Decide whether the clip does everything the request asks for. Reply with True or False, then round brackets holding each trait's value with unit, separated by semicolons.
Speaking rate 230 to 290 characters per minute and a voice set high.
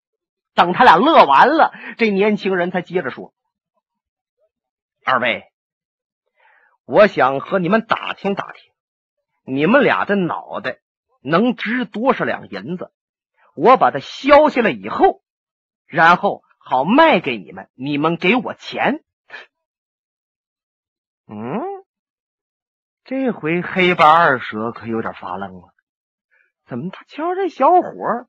False (170 characters per minute; 215 Hz)